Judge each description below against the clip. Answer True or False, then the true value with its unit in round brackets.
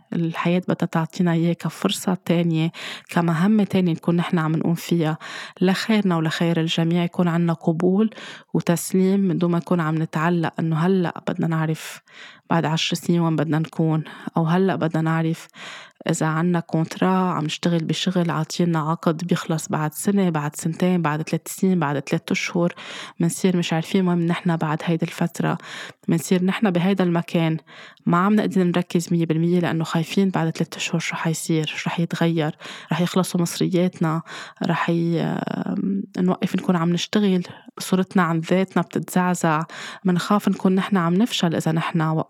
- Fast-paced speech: True (150 wpm)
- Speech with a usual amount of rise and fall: False (2.3 semitones)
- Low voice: False (175 Hz)